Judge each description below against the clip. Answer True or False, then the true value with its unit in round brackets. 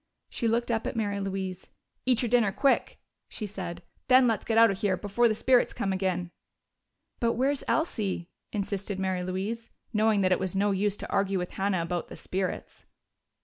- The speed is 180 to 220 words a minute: True (190 wpm)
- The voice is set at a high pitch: True (200 Hz)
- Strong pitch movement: False (3.3 semitones)